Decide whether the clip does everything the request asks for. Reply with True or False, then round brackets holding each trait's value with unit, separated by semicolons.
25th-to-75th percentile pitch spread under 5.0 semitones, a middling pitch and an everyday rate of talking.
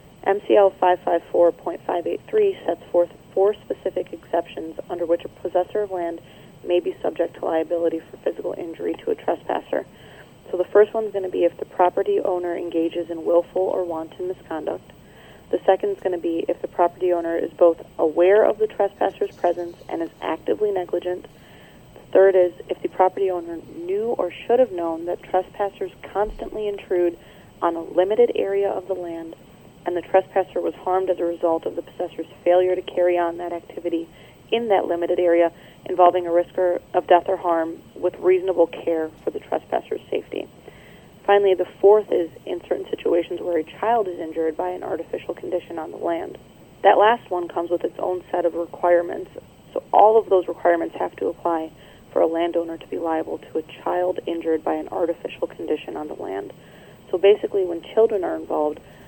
True (2.6 semitones; 180 Hz; 190 wpm)